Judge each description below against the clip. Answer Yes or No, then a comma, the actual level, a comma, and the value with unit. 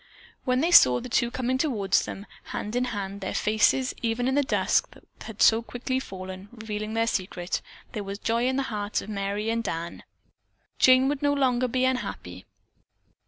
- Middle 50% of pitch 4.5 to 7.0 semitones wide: No, average, 4.1 semitones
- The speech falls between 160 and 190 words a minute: Yes, average, 185 wpm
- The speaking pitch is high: Yes, high, 230 Hz